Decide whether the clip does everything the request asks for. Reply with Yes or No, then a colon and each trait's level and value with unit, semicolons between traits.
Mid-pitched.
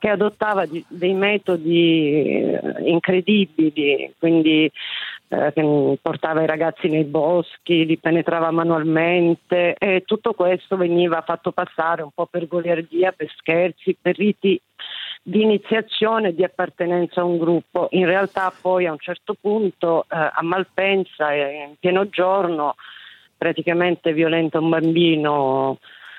Yes: medium, 170 Hz